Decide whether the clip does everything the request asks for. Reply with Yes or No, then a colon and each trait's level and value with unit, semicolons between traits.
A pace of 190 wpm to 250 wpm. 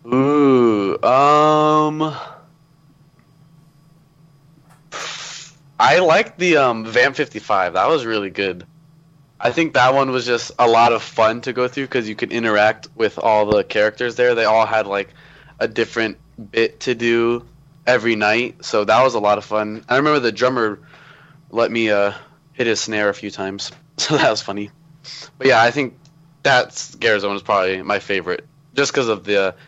No: average, 170 wpm